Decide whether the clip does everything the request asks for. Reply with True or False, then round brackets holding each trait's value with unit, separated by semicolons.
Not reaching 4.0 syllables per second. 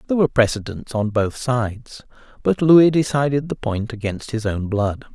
False (5.3 syllables/s)